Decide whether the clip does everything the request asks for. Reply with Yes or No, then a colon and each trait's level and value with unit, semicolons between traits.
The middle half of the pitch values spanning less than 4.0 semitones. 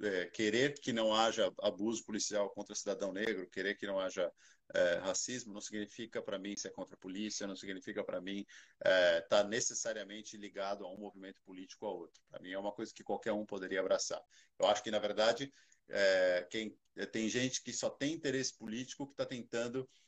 Yes: average, 2.7 semitones